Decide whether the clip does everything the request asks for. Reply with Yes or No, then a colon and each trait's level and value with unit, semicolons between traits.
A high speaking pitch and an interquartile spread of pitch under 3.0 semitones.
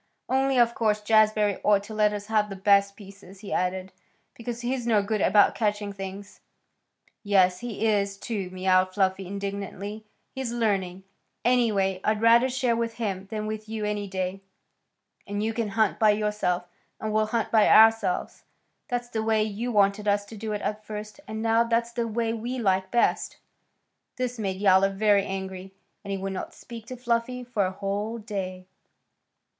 Yes: high, 210 Hz; narrow, 2.5 semitones